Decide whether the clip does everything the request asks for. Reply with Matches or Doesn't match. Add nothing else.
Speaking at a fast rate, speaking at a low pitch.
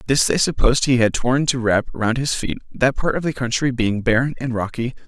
Matches